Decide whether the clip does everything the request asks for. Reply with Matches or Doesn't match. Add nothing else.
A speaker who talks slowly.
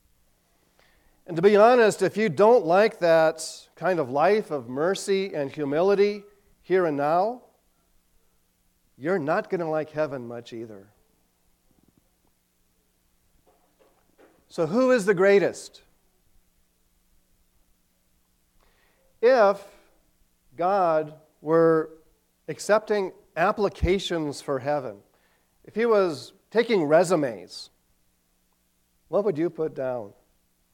Matches